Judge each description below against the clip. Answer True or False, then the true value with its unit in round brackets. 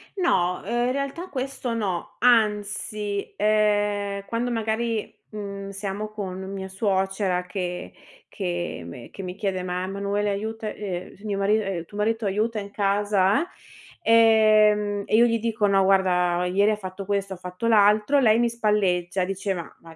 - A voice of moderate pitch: False (205 Hz)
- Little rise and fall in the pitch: True (2.3 semitones)